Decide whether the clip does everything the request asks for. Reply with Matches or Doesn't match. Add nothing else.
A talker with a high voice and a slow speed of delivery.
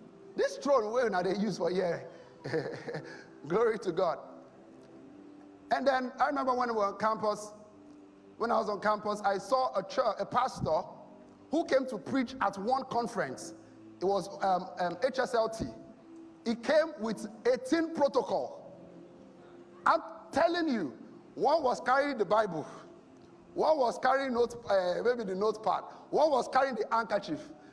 Doesn't match